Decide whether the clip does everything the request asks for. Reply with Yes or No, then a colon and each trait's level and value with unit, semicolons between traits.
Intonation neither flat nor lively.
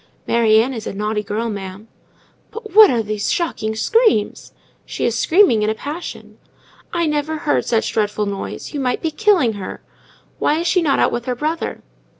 No: wide, 6.9 semitones